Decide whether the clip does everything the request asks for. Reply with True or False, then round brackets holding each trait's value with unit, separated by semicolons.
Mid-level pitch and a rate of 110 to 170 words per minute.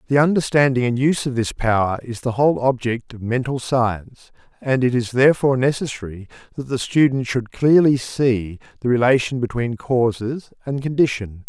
False (125 Hz; 160 wpm)